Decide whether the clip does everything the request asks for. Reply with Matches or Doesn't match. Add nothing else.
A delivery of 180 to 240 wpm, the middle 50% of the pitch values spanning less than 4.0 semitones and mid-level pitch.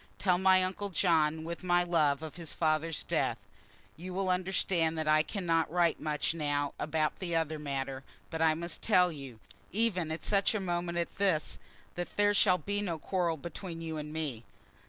Matches